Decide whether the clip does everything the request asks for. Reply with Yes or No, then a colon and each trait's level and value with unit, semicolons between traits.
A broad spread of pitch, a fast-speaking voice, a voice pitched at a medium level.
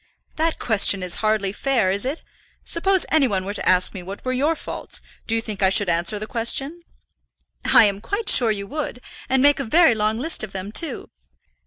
No: wide, 5.9 semitones; fast, 210 wpm; high, 225 Hz